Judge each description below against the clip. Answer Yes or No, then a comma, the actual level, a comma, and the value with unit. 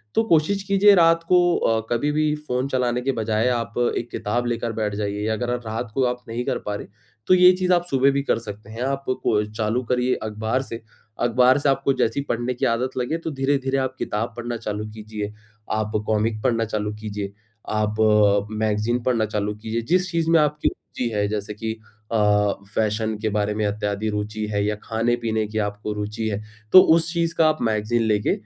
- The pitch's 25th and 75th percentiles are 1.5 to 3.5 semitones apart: No, average, 3.9 semitones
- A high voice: No, low, 115 Hz